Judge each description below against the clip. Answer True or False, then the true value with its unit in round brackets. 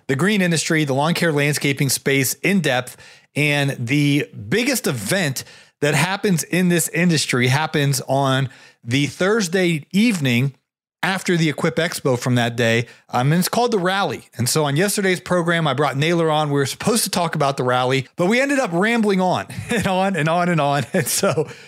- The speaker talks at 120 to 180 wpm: False (190 wpm)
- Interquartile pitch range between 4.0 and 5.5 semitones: True (5.1 semitones)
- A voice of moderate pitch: True (155 Hz)